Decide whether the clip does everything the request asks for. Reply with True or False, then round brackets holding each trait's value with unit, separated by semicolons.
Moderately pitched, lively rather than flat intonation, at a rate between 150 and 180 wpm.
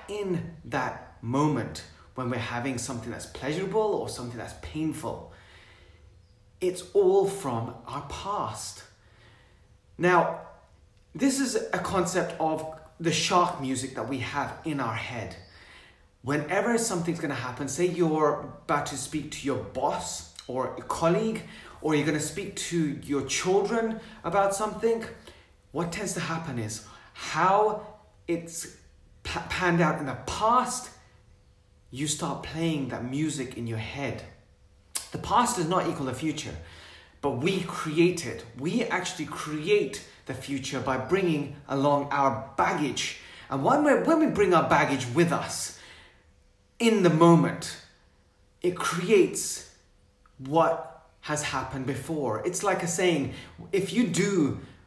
False (145 Hz; 7.3 semitones; 140 wpm)